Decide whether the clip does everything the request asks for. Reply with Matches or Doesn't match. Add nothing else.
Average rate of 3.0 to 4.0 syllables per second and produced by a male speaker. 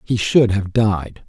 Matches